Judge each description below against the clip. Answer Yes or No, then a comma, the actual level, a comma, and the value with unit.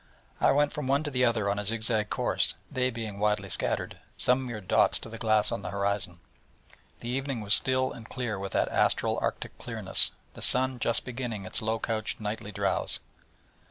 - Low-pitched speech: Yes, low, 115 Hz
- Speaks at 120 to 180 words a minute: No, average, 195 wpm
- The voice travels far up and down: No, average, 3.4 semitones